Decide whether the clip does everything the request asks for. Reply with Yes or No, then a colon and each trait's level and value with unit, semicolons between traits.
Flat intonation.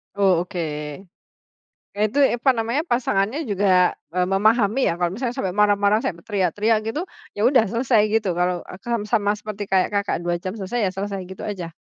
No: average, 3.1 semitones